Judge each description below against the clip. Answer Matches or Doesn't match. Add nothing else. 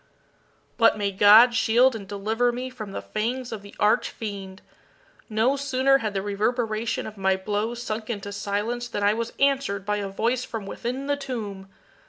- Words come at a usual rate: Matches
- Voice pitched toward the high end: Matches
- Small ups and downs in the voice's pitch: Doesn't match